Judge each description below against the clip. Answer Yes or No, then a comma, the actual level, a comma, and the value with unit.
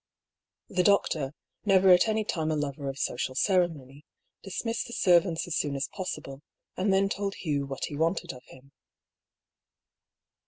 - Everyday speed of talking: Yes, average, 160 wpm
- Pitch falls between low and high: Yes, medium, 165 Hz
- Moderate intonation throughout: No, wide, 5.7 semitones